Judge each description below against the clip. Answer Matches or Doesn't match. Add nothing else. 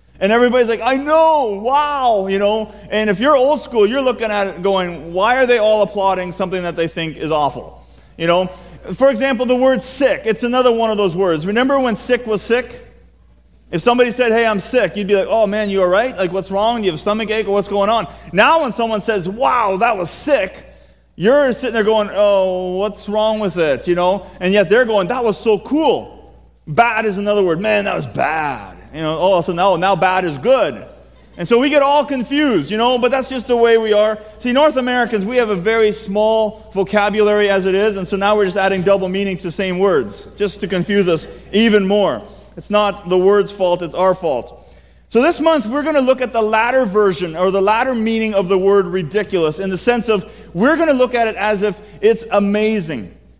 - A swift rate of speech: Matches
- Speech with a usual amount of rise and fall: Matches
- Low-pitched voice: Doesn't match